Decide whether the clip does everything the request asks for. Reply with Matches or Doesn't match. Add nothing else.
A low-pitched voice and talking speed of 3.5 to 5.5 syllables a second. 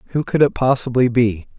Doesn't match